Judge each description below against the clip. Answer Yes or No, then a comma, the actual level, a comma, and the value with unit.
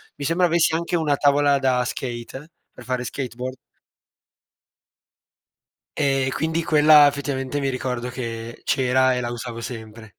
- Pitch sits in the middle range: No, low, 130 Hz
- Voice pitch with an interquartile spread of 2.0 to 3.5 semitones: Yes, average, 2.7 semitones